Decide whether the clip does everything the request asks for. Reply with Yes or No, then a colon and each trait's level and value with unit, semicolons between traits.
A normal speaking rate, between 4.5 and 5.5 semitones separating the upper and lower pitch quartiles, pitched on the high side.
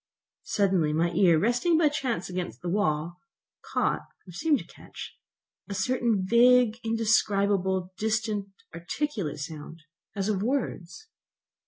No: slow, 120 wpm; average, 5.1 semitones; high, 200 Hz